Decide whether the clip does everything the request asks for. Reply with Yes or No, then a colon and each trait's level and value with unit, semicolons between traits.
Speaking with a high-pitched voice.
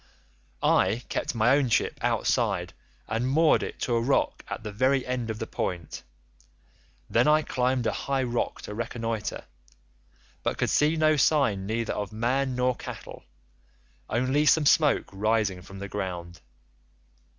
No: low, 120 Hz